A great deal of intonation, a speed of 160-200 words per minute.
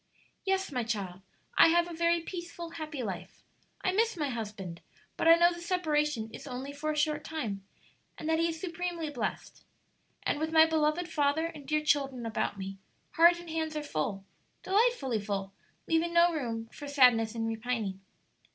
Yes: wide, 6.8 semitones; average, 180 wpm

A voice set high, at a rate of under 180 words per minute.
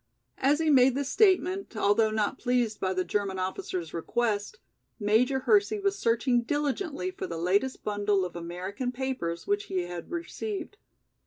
Yes: high, 235 Hz; average, 155 wpm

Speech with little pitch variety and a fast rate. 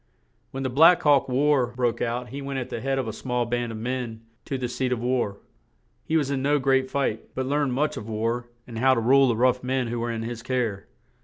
Yes: narrow, 2.2 semitones; fast, 245 wpm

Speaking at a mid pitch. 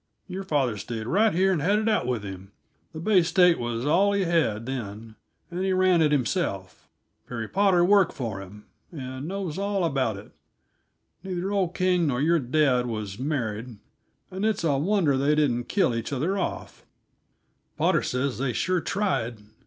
Yes: medium, 150 Hz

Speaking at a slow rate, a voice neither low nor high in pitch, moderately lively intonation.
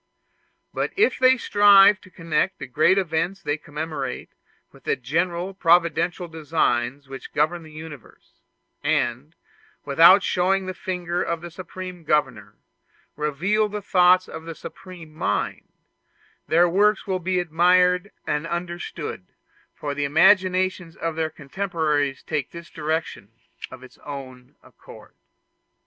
Yes: slow, 130 wpm; medium, 170 Hz; average, 3.4 semitones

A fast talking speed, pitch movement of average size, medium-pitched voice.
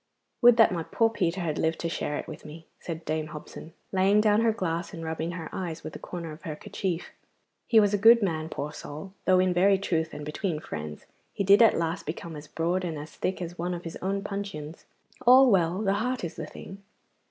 Yes: fast, 230 wpm; average, 3.7 semitones; medium, 175 Hz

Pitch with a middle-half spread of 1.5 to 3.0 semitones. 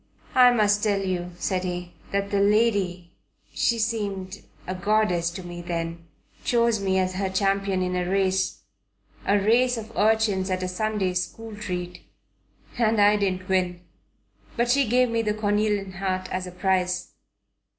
Yes: average, 2.7 semitones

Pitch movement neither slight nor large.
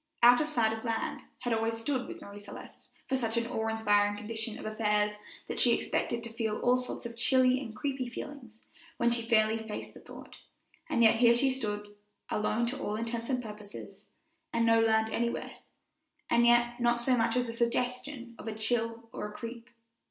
No: narrow, 1.6 semitones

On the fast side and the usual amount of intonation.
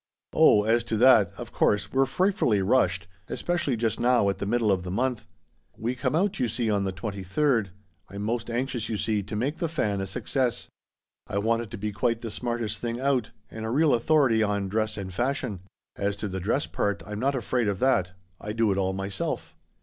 Yes: fast, 225 wpm; average, 3.8 semitones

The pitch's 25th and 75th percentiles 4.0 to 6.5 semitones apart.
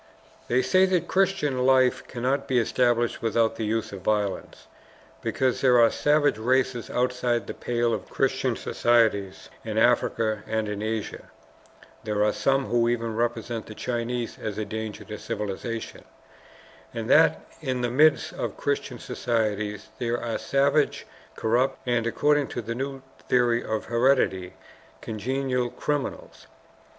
No: average, 2.8 semitones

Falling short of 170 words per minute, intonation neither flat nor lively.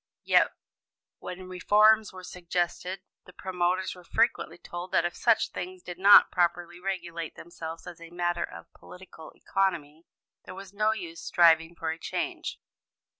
No: average, 150 wpm; narrow, 1.7 semitones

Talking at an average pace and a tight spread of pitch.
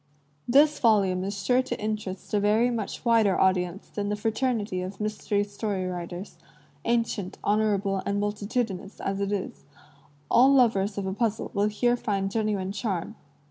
Yes: average, 160 wpm; narrow, 2.3 semitones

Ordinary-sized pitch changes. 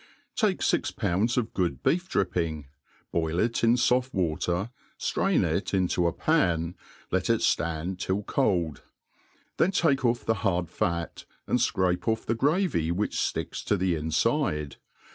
No: wide, 5.7 semitones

